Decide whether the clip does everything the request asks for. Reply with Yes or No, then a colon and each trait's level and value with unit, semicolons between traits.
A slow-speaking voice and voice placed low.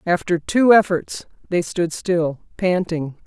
No: slow, 130 wpm; medium, 175 Hz